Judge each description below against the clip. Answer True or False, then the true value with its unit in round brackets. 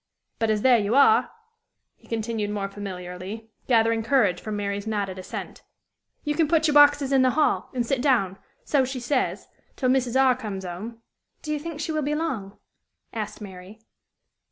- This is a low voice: False (230 Hz)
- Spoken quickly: False (175 wpm)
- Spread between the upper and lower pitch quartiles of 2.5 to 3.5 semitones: False (5.1 semitones)